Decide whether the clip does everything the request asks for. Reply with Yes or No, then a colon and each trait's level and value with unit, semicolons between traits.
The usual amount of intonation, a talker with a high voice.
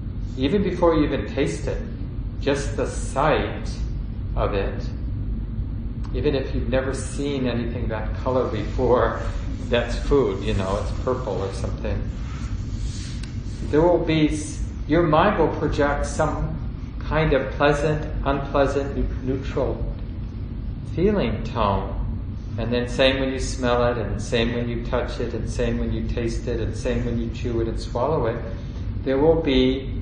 No: average, 3.6 semitones; low, 120 Hz